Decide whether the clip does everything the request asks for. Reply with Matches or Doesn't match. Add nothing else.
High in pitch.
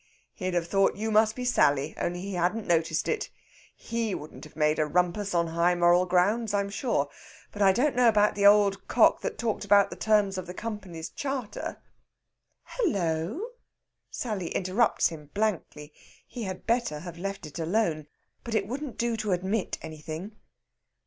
Matches